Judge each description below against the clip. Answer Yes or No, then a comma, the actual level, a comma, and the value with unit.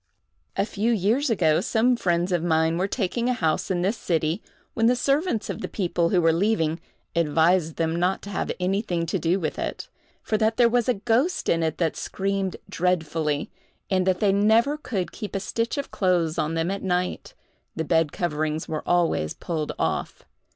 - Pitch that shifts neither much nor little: Yes, average, 4.9 semitones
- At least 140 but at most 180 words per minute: No, average, 190 wpm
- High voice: No, medium, 180 Hz